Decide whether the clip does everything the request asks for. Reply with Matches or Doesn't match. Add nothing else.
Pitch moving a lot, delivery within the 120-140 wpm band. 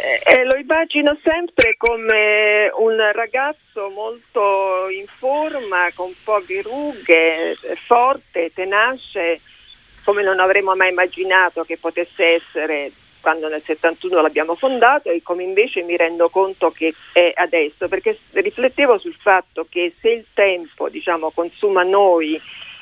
Matches